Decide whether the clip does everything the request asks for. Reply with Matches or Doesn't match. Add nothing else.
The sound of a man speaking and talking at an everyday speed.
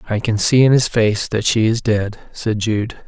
Doesn't match